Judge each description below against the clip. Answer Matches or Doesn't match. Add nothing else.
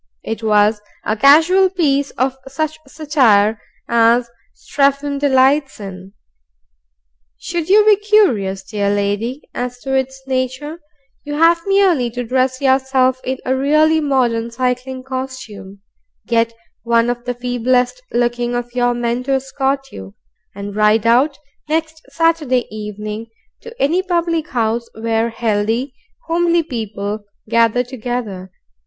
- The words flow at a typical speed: Doesn't match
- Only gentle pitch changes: Doesn't match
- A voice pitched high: Matches